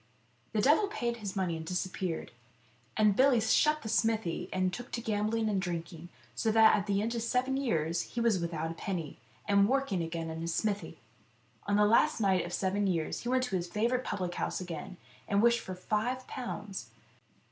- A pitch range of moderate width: Yes, average, 4.7 semitones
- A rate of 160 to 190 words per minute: No, average, 200 wpm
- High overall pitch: Yes, high, 205 Hz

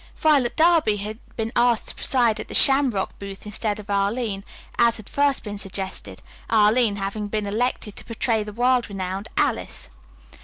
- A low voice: No, high, 215 Hz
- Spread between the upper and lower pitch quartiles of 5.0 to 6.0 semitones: No, average, 3.3 semitones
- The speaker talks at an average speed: Yes, average, 175 wpm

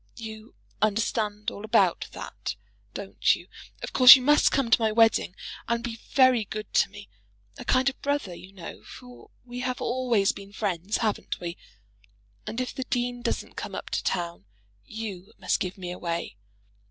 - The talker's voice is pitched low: No, high, 220 Hz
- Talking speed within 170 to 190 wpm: Yes, average, 175 wpm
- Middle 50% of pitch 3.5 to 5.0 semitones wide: Yes, average, 3.9 semitones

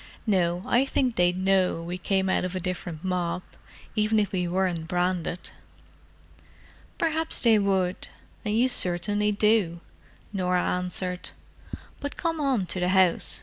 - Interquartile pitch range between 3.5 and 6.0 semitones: No, average, 2.8 semitones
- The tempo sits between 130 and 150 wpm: Yes, average, 140 wpm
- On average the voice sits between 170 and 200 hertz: Yes, medium, 185 Hz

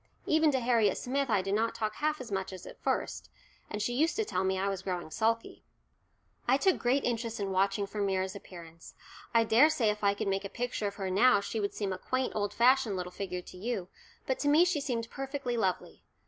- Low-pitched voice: No, high, 215 Hz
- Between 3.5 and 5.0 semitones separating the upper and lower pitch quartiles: Yes, average, 4.6 semitones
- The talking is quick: Yes, fast, 230 wpm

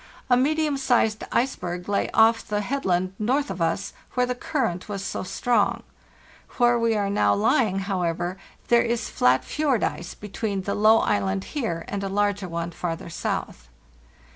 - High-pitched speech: Yes, high, 205 Hz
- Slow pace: No, average, 165 wpm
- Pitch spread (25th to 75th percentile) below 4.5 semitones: No, average, 5.2 semitones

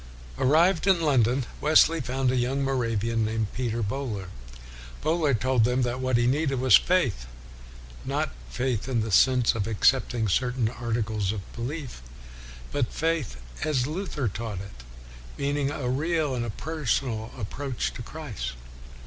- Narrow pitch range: No, average, 4.0 semitones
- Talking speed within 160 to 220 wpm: No, average, 150 wpm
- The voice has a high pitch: No, low, 125 Hz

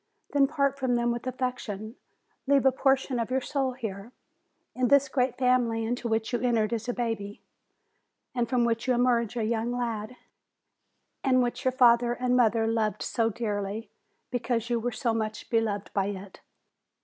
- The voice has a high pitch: Yes, high, 240 Hz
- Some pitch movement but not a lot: No, narrow, 2.2 semitones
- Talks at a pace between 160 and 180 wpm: Yes, average, 175 wpm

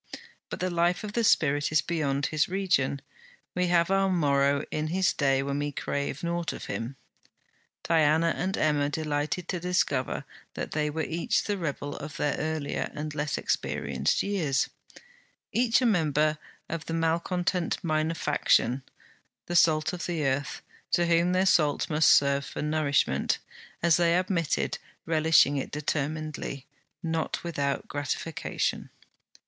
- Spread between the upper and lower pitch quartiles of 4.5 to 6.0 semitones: No, average, 3.1 semitones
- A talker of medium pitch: Yes, medium, 155 Hz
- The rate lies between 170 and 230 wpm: No, average, 145 wpm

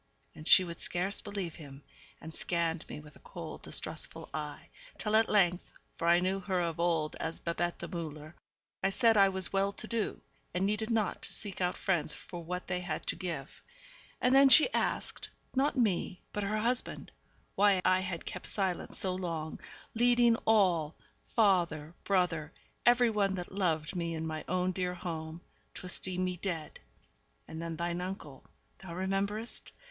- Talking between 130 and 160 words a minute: No, average, 175 wpm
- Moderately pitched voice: Yes, medium, 180 Hz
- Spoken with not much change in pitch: No, average, 3.1 semitones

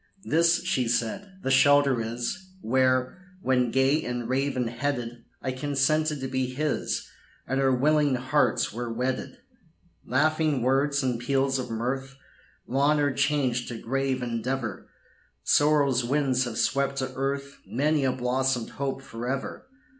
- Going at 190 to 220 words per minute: No, average, 140 wpm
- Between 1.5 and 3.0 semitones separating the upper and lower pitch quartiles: Yes, narrow, 2.4 semitones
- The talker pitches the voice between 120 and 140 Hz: Yes, low, 135 Hz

